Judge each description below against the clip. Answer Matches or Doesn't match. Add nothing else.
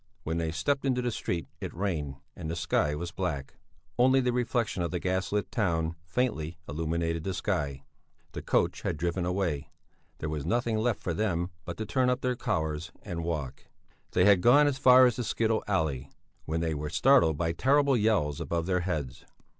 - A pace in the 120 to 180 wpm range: Doesn't match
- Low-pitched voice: Matches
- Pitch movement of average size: Doesn't match